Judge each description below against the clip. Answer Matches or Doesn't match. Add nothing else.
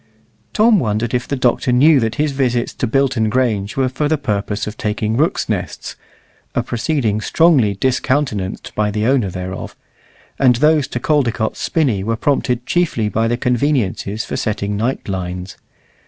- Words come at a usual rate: Matches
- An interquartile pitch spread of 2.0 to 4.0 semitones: Doesn't match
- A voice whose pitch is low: Matches